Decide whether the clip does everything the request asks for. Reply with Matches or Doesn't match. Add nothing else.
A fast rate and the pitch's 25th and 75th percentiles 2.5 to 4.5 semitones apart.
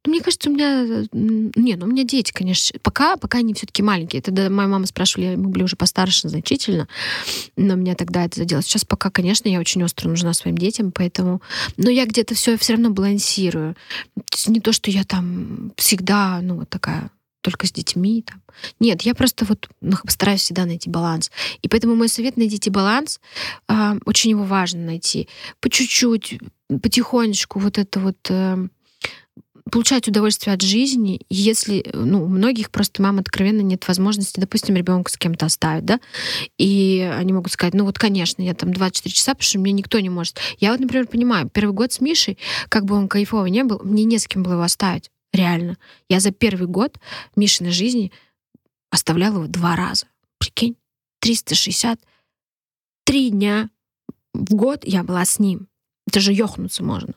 Matches